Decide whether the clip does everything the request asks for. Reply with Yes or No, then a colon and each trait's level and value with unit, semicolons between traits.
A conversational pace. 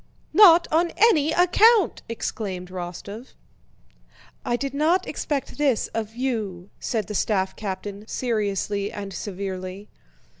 No: slow, 115 wpm